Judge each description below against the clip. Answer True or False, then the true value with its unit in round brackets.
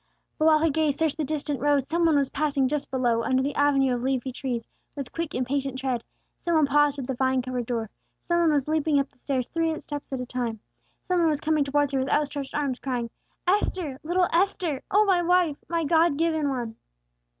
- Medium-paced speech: False (225 wpm)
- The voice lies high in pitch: True (285 Hz)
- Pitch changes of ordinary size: True (3.3 semitones)